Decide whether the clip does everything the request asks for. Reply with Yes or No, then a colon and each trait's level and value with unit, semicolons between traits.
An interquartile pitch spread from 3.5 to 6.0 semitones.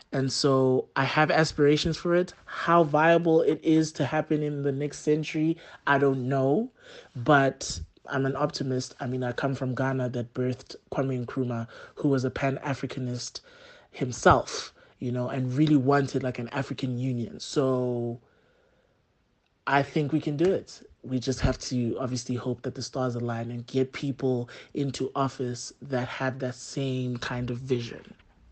No: narrow, 2.5 semitones